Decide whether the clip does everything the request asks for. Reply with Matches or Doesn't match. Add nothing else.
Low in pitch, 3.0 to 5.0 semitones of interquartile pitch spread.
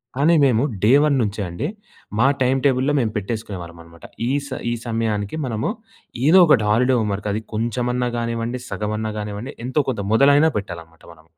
Matches